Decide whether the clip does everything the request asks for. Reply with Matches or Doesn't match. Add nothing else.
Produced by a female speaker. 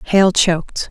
Matches